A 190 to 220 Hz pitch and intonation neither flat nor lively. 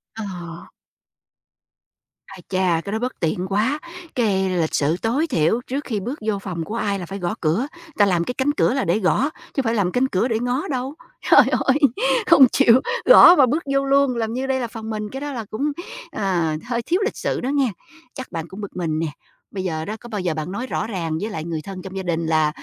No: high, 215 Hz; wide, 6.3 semitones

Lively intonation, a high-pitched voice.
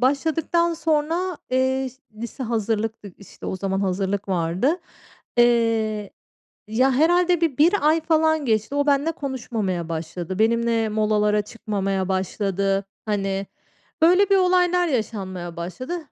Yes: wide, 7.8 semitones; high, 230 Hz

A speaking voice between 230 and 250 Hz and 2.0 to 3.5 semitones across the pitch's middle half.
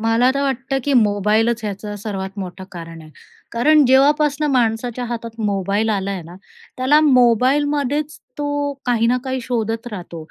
No: high, 235 Hz; average, 4.8 semitones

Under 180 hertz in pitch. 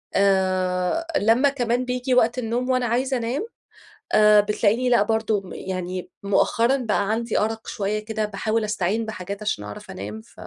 No: high, 220 Hz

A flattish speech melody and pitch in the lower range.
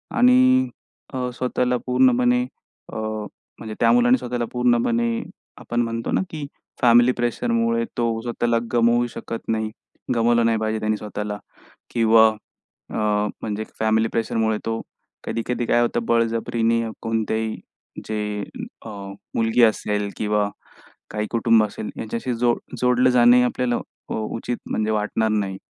Yes: narrow, 1.9 semitones; low, 115 Hz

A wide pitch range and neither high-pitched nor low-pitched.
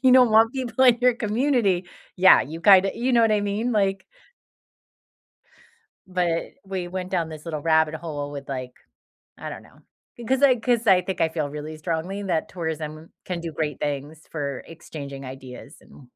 Yes: wide, 5.8 semitones; medium, 175 Hz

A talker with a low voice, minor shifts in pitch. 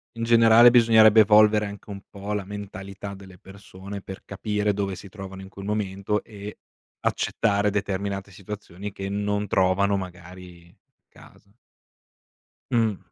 Yes: low, 100 Hz; narrow, 1.5 semitones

